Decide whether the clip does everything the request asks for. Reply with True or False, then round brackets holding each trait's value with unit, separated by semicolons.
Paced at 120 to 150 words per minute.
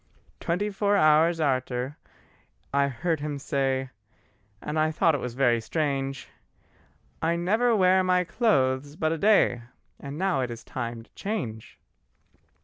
True (140 wpm)